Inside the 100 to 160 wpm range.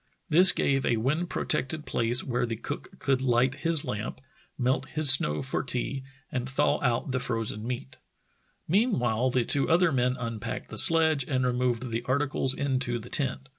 No: average, 170 wpm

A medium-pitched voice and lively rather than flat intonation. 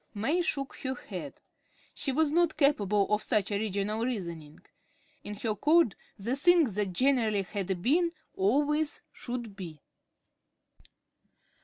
No: high, 225 Hz; wide, 6.3 semitones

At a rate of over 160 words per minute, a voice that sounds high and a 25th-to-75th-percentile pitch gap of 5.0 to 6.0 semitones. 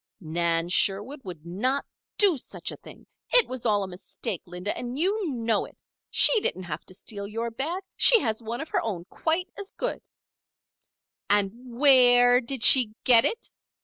Yes: average, 180 wpm; high, 235 Hz; wide, 5.6 semitones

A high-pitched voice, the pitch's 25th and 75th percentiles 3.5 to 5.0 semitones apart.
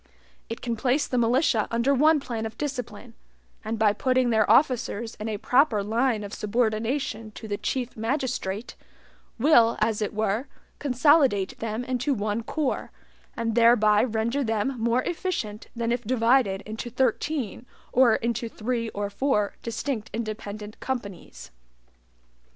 No: high, 230 Hz; average, 3.0 semitones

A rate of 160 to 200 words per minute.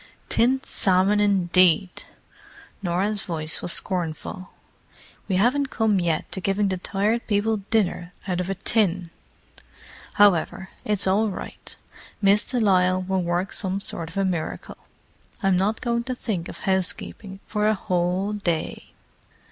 No: average, 140 wpm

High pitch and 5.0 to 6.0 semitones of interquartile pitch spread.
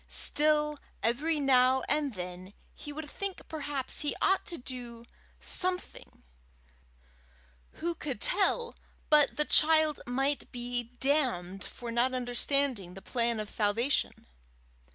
No: very high, 265 Hz; average, 4.1 semitones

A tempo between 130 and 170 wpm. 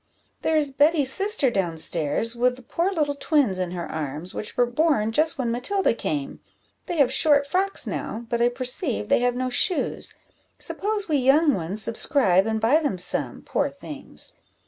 No: average, 180 wpm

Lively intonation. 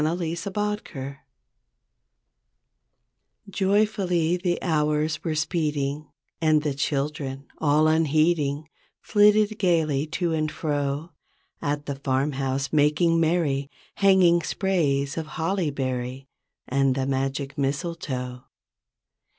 No: average, 3.7 semitones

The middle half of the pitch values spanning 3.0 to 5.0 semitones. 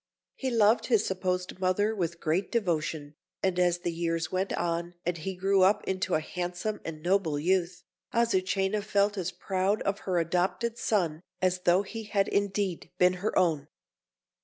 No: narrow, 2.6 semitones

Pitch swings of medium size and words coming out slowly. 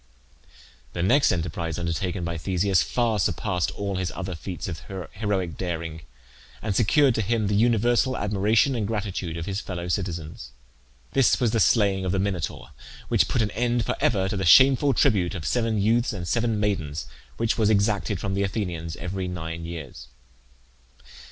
No: average, 4.2 semitones; average, 170 wpm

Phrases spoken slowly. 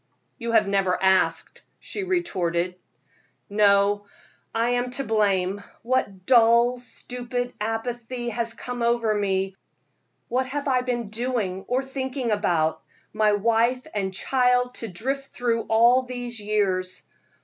Yes: slow, 125 wpm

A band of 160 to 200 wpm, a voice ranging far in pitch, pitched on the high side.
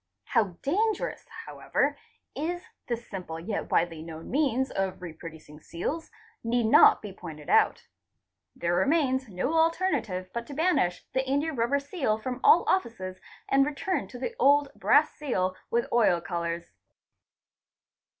No: average, 150 wpm; wide, 7.8 semitones; high, 235 Hz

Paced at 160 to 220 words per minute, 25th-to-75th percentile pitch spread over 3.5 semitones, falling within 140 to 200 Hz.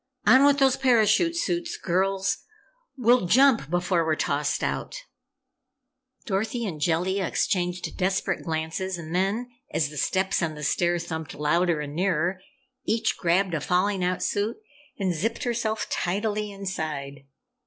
No: average, 140 wpm; average, 4.6 semitones; medium, 185 Hz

